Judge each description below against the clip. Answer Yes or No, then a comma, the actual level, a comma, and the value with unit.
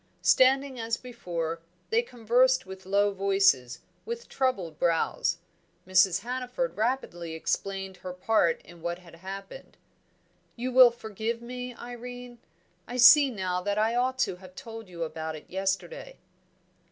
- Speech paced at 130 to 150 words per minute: Yes, average, 140 wpm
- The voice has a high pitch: Yes, high, 215 Hz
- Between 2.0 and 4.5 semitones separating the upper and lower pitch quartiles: No, wide, 5.4 semitones